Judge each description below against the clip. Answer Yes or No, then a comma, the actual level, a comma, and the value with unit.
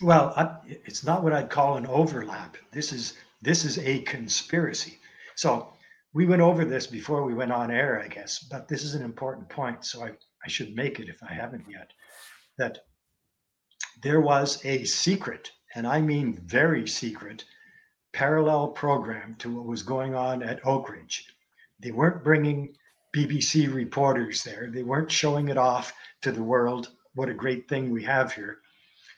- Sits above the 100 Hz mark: Yes, medium, 140 Hz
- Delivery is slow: No, average, 175 wpm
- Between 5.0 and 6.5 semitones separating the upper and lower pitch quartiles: No, average, 3.7 semitones